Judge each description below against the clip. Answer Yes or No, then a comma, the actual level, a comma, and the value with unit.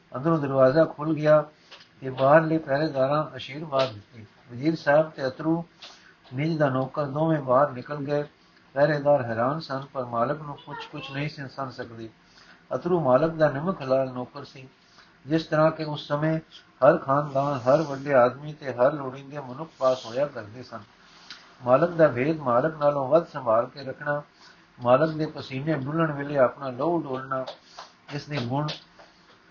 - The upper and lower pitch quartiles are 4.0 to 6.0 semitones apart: No, average, 2.9 semitones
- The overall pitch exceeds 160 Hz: No, medium, 145 Hz